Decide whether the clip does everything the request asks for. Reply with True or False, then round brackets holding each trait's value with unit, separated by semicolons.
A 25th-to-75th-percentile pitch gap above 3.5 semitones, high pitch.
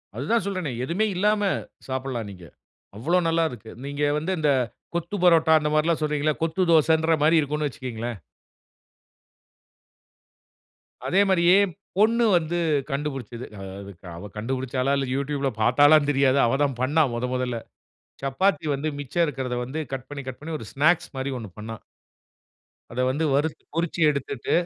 False (4.0 semitones; 145 Hz)